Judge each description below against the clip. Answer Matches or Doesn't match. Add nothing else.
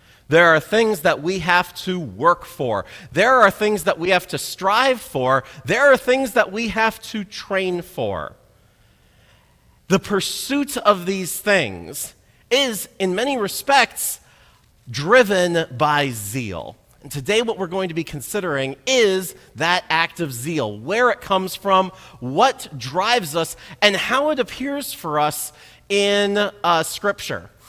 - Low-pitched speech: Doesn't match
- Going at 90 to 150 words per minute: Matches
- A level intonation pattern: Doesn't match